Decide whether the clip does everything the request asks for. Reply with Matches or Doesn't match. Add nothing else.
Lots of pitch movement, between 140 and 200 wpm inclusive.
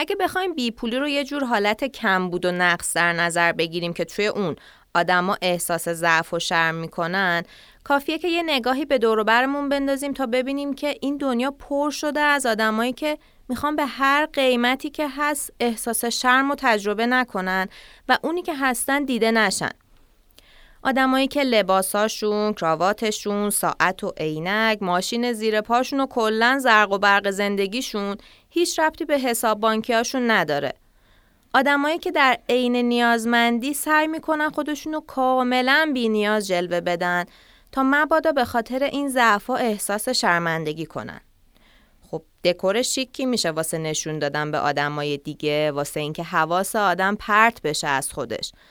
Matches